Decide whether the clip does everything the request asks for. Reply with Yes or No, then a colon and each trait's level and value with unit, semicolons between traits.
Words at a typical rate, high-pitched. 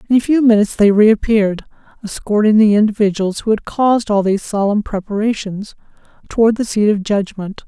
Yes: average, 165 wpm; high, 210 Hz